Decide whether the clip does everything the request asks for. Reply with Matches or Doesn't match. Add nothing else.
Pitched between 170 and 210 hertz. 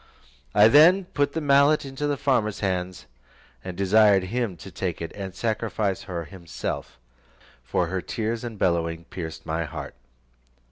Doesn't match